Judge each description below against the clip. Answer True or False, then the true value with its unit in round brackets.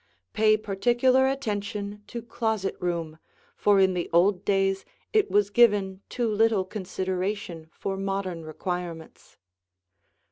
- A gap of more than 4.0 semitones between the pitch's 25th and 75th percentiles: False (2.6 semitones)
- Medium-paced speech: False (115 wpm)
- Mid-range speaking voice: False (195 Hz)